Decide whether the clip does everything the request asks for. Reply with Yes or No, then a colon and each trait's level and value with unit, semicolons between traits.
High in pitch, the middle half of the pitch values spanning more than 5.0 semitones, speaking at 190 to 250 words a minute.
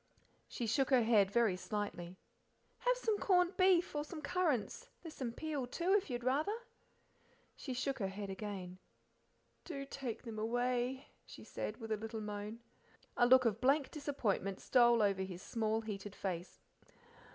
No: high, 240 Hz; wide, 5.4 semitones; average, 160 wpm